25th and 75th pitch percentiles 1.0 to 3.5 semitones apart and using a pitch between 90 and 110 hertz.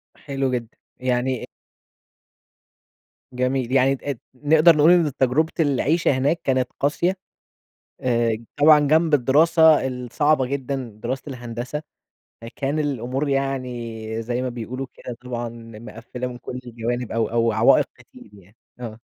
No: average, 3.2 semitones; low, 130 Hz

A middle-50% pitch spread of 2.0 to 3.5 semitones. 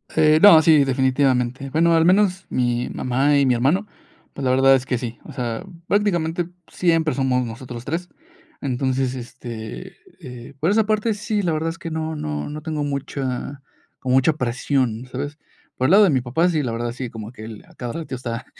No: average, 4.5 semitones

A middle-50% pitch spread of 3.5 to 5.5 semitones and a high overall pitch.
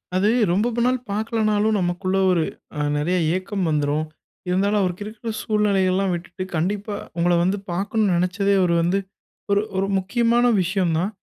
No: average, 2.8 semitones; high, 195 Hz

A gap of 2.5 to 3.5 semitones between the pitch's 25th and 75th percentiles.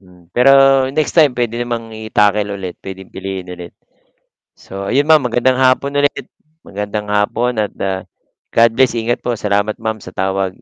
No: average, 4.1 semitones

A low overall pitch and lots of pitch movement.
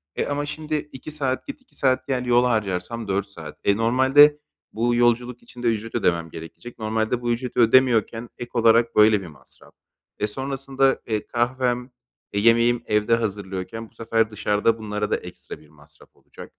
No: low, 115 Hz; average, 3.0 semitones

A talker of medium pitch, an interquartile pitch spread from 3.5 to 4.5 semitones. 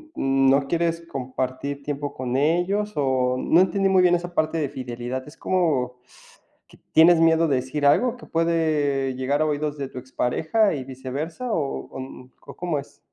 Yes: medium, 145 Hz; average, 4.1 semitones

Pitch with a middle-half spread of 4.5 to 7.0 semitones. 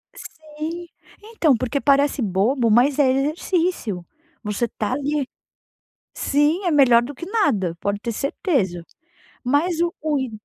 Yes: average, 5.1 semitones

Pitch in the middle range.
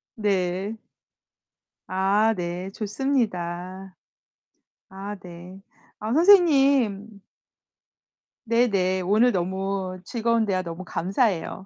No: high, 195 Hz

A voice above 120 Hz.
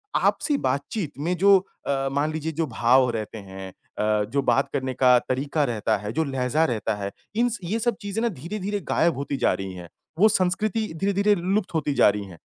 Yes: medium, 140 Hz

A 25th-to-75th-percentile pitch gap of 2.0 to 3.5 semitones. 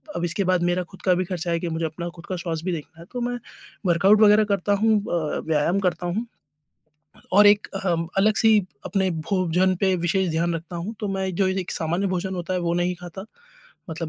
Yes: narrow, 2.4 semitones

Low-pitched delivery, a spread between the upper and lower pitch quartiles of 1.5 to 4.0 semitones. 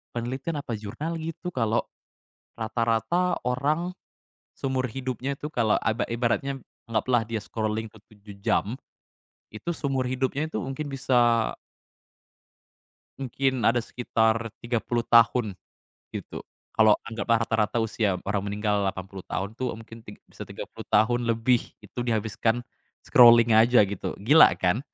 Yes: low, 115 Hz; average, 2.9 semitones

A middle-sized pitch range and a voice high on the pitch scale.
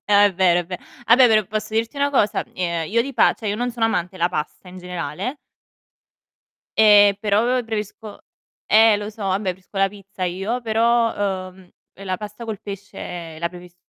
Yes: average, 3.2 semitones; high, 205 Hz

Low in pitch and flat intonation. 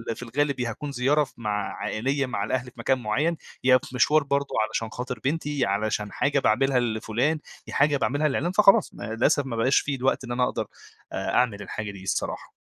No: low, 130 Hz; average, 4.0 semitones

